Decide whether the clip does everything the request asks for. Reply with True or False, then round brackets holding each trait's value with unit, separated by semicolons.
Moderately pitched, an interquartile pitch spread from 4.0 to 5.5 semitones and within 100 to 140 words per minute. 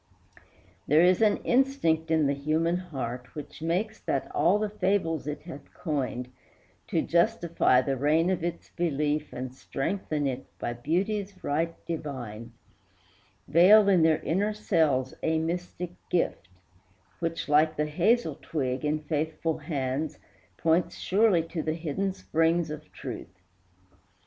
False (160 Hz; 3.5 semitones; 135 wpm)